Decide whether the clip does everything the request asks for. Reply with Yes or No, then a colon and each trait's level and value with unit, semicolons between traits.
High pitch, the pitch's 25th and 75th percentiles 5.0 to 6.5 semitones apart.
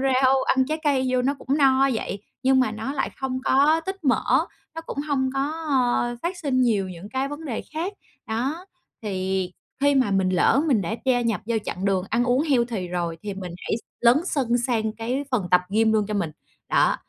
No: very high, 250 Hz; average, 4.4 semitones